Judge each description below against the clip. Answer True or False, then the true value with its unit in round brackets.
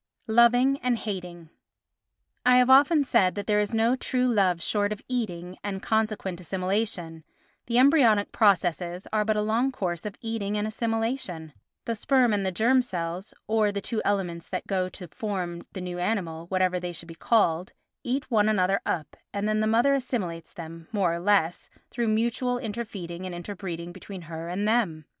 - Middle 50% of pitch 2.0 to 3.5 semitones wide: False (4.3 semitones)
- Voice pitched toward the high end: True (205 Hz)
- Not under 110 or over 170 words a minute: False (180 wpm)